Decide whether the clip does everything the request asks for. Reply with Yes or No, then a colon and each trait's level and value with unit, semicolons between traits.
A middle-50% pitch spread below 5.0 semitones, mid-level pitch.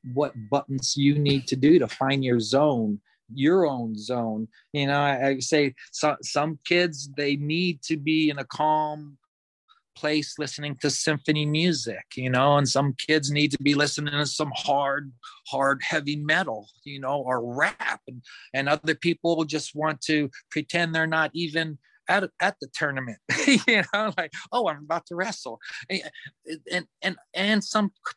Yes: average, 2.7 semitones; medium, 150 Hz